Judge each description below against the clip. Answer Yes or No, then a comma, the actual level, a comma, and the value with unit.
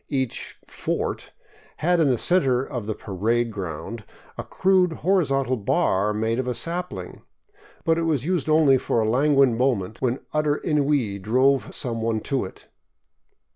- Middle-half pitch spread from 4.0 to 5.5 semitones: Yes, average, 5.2 semitones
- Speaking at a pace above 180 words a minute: No, average, 175 wpm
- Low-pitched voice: Yes, low, 130 Hz